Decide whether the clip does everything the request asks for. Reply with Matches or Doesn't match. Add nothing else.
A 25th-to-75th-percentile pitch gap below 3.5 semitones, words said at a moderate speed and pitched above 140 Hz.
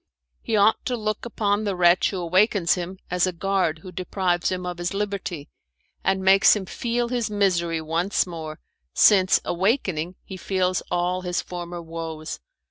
Matches